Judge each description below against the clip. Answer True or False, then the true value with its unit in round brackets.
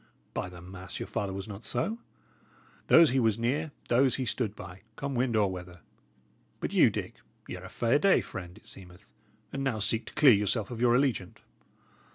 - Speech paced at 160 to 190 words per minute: False (200 wpm)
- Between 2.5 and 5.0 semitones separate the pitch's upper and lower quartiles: False (5.4 semitones)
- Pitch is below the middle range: True (110 Hz)